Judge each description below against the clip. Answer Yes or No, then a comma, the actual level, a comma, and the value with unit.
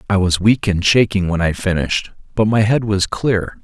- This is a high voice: No, low, 100 Hz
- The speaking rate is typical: No, fast, 215 wpm